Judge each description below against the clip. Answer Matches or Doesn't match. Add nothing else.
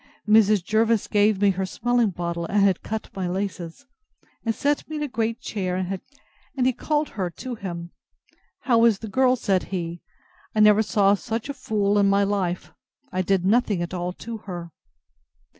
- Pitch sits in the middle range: Doesn't match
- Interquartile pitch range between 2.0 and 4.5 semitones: Matches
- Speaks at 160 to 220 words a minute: Matches